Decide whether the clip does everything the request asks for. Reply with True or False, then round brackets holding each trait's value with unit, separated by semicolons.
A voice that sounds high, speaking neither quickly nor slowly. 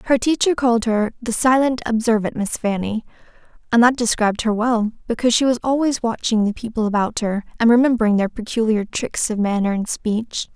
True (230 Hz; 180 wpm)